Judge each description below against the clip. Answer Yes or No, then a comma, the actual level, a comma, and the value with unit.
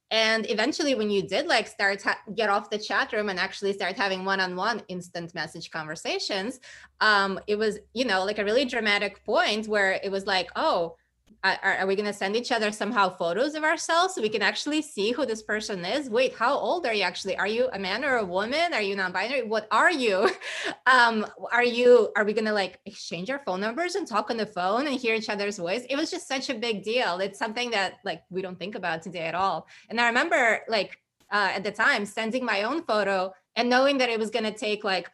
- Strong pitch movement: No, average, 4.2 semitones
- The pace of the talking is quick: Yes, fast, 235 wpm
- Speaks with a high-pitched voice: Yes, high, 210 Hz